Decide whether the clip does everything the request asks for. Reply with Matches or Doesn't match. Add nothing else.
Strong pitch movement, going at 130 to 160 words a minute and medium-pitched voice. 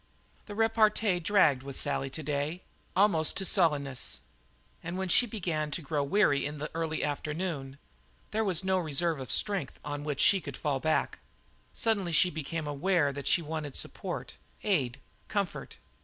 Doesn't match